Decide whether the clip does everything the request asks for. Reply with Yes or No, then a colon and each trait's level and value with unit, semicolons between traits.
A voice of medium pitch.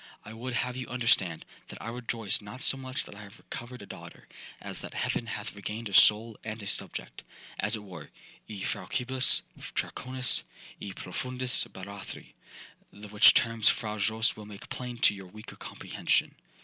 No: low, 110 Hz